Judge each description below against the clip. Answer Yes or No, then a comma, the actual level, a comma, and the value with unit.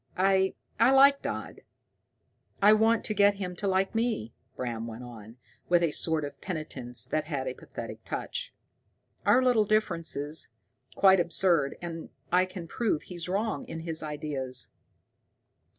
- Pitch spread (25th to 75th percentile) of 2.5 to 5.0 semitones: No, wide, 5.6 semitones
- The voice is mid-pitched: Yes, medium, 175 Hz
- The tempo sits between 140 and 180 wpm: Yes, average, 150 wpm